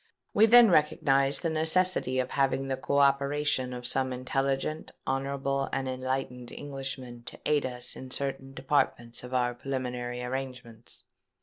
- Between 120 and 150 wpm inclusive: Yes, average, 140 wpm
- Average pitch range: No, narrow, 1.7 semitones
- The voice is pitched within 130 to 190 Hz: Yes, low, 135 Hz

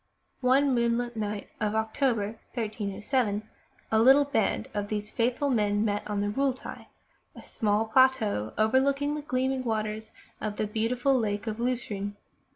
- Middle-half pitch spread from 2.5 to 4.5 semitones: Yes, average, 3.6 semitones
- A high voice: Yes, high, 220 Hz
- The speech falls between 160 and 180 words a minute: No, average, 150 wpm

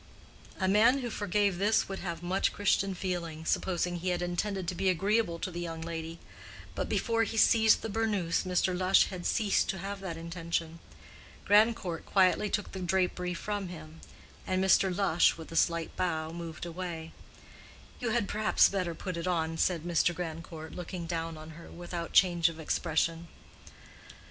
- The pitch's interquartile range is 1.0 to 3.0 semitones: Yes, average, 2.7 semitones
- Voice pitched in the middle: Yes, medium, 180 Hz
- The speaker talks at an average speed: Yes, average, 170 wpm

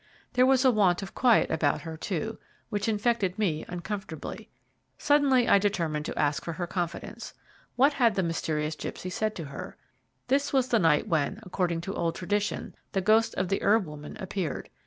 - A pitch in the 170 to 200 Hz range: Yes, high, 190 Hz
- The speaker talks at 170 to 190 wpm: Yes, average, 180 wpm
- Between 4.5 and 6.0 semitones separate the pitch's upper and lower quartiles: Yes, average, 5.1 semitones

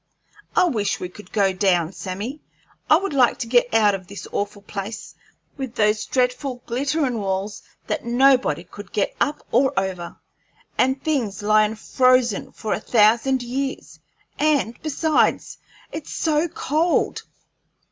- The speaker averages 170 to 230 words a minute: No, average, 140 wpm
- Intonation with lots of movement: No, average, 4.8 semitones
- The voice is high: Yes, high, 235 Hz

